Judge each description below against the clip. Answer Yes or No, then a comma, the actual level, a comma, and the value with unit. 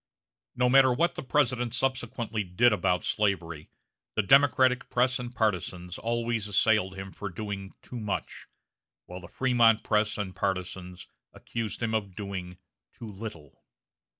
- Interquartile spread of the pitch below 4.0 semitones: No, average, 4.3 semitones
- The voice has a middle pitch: No, low, 110 Hz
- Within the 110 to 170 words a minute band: Yes, average, 140 wpm